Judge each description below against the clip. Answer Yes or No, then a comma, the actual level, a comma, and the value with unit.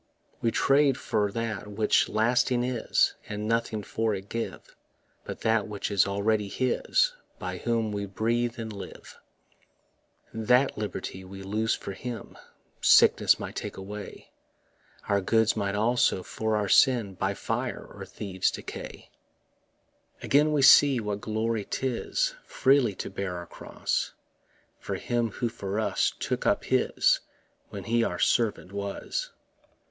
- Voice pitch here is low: Yes, low, 110 Hz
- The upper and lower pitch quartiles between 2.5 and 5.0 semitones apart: Yes, average, 2.9 semitones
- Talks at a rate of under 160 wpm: Yes, average, 140 wpm